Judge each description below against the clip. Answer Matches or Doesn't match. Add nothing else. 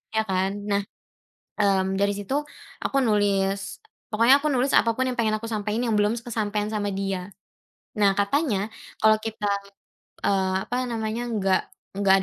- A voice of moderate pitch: Doesn't match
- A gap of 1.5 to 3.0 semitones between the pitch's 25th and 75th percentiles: Matches